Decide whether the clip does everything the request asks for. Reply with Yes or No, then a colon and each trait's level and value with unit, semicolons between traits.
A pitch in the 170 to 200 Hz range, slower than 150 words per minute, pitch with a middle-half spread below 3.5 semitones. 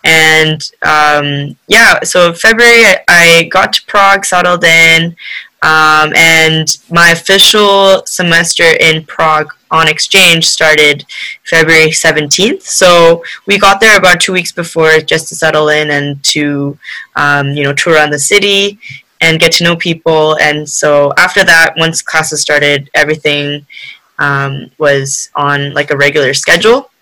No: medium, 160 Hz; average, 140 wpm; average, 2.7 semitones